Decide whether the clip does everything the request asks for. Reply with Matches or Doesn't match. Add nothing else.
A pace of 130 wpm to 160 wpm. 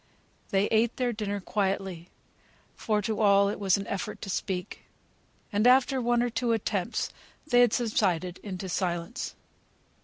Matches